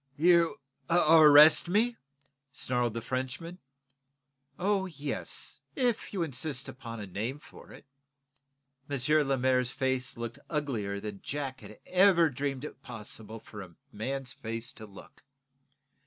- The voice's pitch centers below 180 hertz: Yes, low, 135 Hz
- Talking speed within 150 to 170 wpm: No, slow, 135 wpm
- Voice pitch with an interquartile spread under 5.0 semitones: No, average, 5.3 semitones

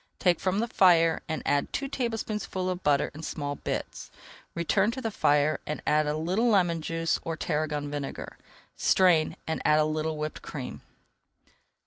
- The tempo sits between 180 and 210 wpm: No, average, 165 wpm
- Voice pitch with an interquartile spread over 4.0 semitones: No, average, 3.7 semitones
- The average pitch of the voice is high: No, medium, 165 Hz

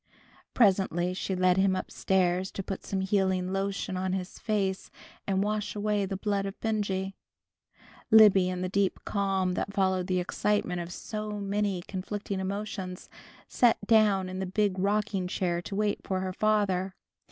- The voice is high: Yes, high, 195 Hz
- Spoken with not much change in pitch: Yes, narrow, 1.8 semitones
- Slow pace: No, average, 165 wpm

